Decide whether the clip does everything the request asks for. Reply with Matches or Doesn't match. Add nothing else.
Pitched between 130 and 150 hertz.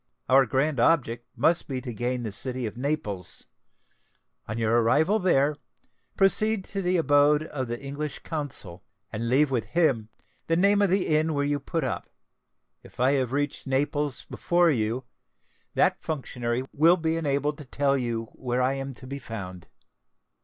Matches